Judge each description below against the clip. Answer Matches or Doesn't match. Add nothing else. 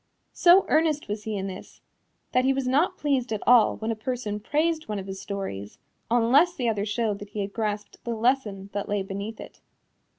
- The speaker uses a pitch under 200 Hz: Doesn't match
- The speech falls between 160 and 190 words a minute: Doesn't match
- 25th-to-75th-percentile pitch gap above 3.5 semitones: Matches